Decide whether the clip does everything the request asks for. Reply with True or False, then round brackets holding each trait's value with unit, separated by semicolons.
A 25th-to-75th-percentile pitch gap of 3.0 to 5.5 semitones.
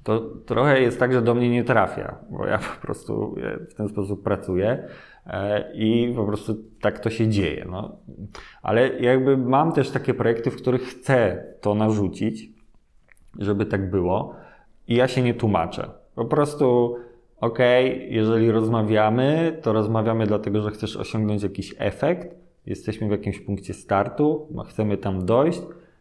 True (3.3 semitones)